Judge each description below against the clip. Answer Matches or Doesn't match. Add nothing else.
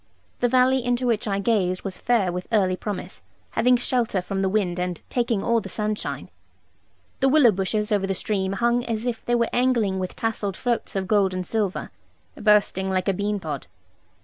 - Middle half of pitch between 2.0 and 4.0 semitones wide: Matches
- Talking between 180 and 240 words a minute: Matches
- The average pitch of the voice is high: Matches